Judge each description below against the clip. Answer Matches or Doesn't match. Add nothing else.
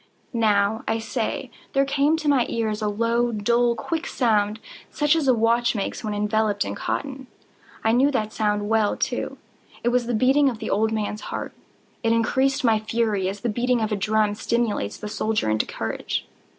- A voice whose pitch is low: Doesn't match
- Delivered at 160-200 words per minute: Matches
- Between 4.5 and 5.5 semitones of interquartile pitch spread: Doesn't match